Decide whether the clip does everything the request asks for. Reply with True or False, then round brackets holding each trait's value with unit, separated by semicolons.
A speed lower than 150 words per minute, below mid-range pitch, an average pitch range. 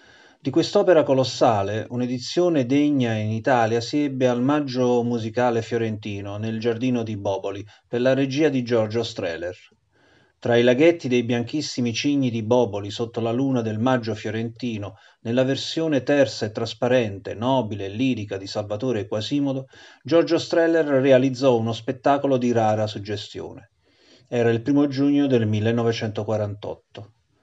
True (135 wpm; 120 Hz; 3.3 semitones)